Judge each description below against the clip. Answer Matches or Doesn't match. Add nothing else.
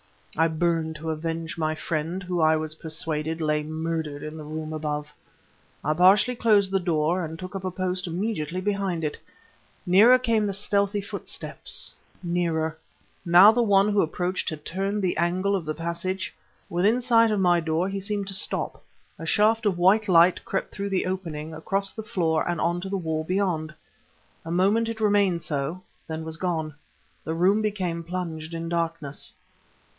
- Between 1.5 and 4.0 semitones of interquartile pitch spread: Matches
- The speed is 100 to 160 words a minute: Doesn't match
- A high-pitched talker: Doesn't match